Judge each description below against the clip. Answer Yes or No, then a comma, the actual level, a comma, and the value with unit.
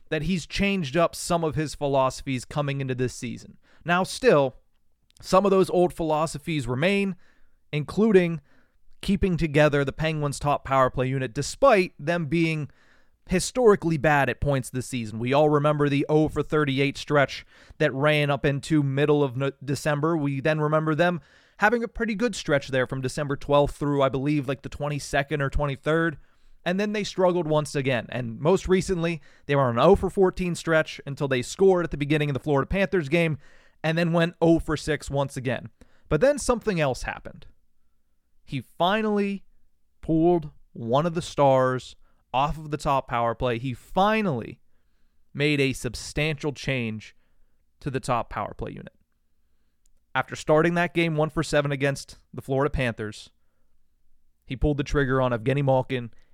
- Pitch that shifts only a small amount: No, average, 4.1 semitones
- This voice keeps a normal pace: Yes, average, 170 wpm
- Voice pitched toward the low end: No, medium, 145 Hz